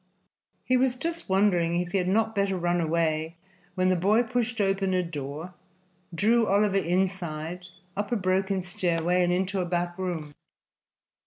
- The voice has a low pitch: No, medium, 185 Hz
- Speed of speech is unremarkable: Yes, average, 160 wpm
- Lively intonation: No, narrow, 2.5 semitones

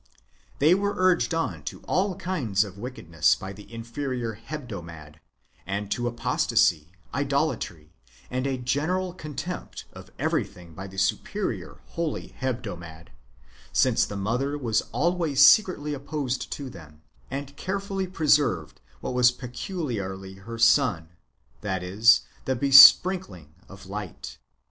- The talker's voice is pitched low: Yes, low, 125 Hz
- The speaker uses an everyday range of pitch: No, wide, 7.6 semitones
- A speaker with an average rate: No, slow, 125 wpm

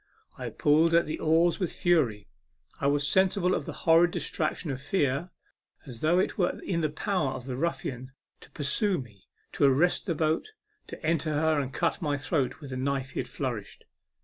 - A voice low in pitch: No, medium, 155 Hz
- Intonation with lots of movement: No, average, 3.7 semitones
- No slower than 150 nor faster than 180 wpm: No, average, 195 wpm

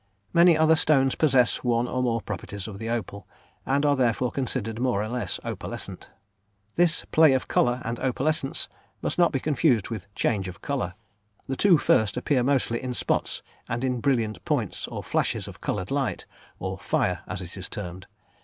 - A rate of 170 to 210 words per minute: Yes, average, 180 wpm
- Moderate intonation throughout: Yes, average, 4.0 semitones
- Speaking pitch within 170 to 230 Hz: No, low, 125 Hz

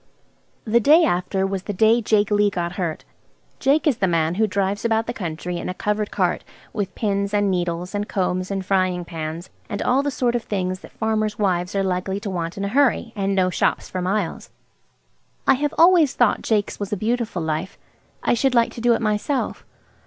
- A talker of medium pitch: No, high, 200 Hz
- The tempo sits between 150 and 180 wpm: No, fast, 205 wpm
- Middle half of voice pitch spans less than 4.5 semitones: Yes, average, 3.6 semitones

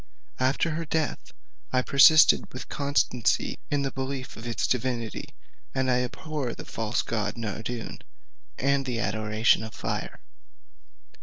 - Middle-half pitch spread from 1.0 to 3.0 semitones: No, average, 3.4 semitones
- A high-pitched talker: No, low, 130 Hz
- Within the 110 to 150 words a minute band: Yes, slow, 135 wpm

